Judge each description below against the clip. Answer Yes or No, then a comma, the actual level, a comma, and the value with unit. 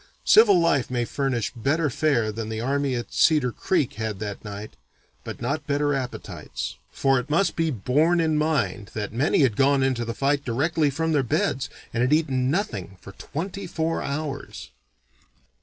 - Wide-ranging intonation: No, average, 4.8 semitones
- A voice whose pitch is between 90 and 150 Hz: Yes, medium, 140 Hz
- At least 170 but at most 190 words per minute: Yes, average, 175 wpm